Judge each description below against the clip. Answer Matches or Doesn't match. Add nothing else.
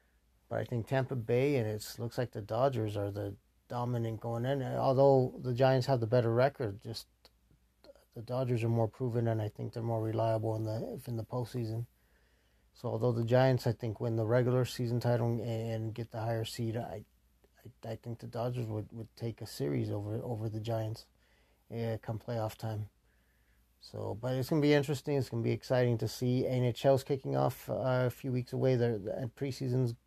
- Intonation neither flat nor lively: Doesn't match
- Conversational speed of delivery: Matches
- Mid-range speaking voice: Doesn't match